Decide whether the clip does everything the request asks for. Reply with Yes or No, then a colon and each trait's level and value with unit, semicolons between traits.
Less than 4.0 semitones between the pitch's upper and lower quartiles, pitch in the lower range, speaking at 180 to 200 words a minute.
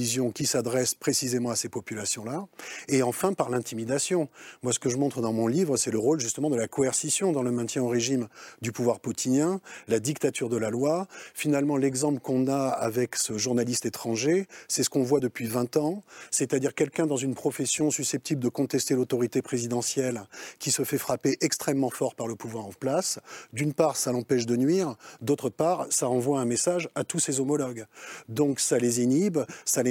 Yes: average, 3.4 semitones; low, 130 Hz; average, 195 wpm